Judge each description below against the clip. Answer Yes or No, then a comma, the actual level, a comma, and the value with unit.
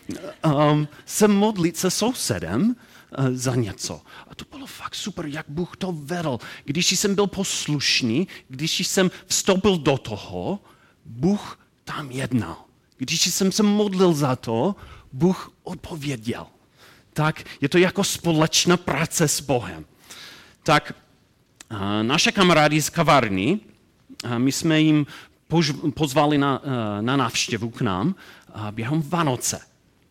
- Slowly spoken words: No, average, 130 wpm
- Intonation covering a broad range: Yes, wide, 6.0 semitones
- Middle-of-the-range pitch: Yes, medium, 150 Hz